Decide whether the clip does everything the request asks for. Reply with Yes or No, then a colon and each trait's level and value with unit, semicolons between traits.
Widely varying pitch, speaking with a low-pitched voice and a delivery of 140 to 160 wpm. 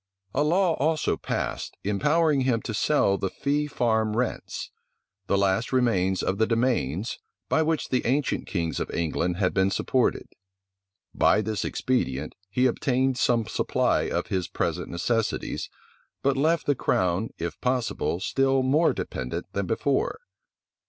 Yes: wide, 5.8 semitones; low, 120 Hz; average, 145 wpm